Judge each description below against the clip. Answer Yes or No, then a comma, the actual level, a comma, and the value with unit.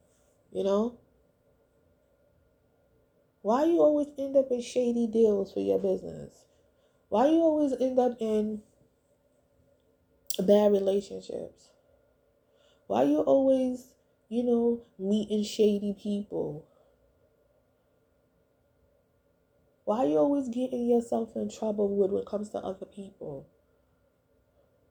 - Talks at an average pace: No, slow, 105 wpm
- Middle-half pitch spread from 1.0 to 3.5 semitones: No, average, 4.1 semitones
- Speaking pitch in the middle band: No, high, 220 Hz